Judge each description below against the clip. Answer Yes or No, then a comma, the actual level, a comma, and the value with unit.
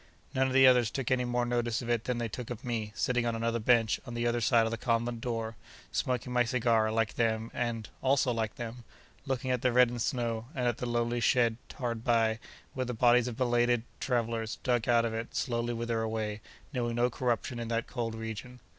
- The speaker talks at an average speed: No, fast, 210 wpm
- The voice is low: Yes, low, 120 Hz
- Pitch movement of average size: No, narrow, 1.4 semitones